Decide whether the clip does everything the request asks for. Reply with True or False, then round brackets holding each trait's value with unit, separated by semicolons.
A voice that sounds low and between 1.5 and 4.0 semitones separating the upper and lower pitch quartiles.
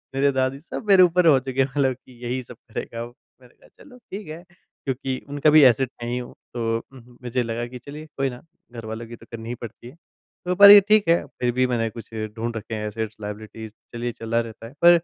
True (125 Hz; 3.3 semitones)